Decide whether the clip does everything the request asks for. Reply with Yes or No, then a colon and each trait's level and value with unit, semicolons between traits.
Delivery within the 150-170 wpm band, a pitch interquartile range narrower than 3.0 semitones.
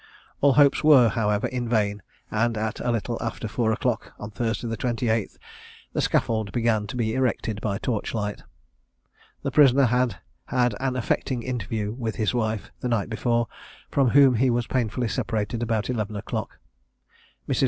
Yes: average, 165 wpm; narrow, 2.4 semitones